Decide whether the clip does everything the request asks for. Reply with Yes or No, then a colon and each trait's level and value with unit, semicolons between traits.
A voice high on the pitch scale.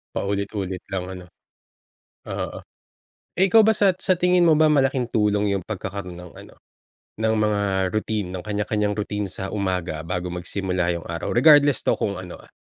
No: low, 100 Hz